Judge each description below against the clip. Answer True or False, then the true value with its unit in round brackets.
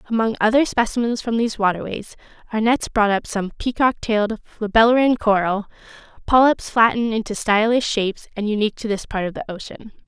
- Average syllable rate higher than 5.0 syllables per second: True (6.0 syllables/s)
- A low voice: False (220 Hz)